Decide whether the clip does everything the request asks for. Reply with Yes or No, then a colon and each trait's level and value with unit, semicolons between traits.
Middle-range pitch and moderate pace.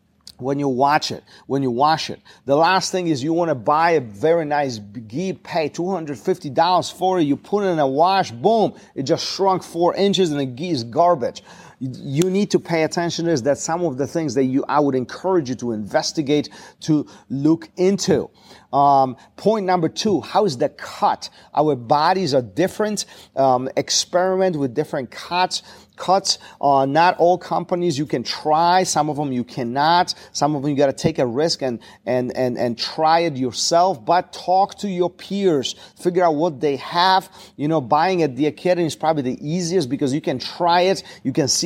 Yes: medium, 160 Hz; average, 195 wpm